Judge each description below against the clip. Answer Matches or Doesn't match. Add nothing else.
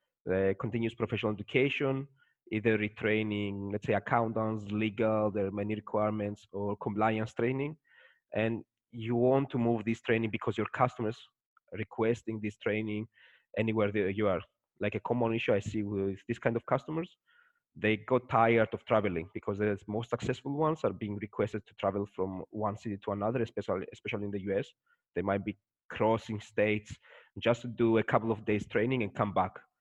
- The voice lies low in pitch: Matches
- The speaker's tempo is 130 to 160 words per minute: Doesn't match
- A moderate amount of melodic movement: Doesn't match